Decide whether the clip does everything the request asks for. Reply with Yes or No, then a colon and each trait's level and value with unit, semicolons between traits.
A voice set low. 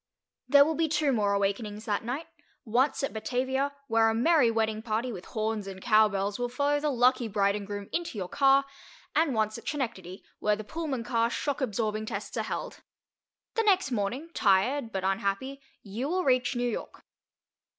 No: high, 230 Hz